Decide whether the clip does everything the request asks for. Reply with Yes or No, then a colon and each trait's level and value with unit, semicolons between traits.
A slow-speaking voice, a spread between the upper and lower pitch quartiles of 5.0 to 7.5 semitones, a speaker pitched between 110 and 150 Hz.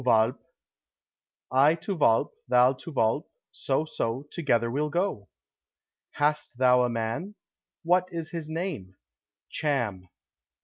Yes: slow, 125 wpm; wide, 5.4 semitones; low, 135 Hz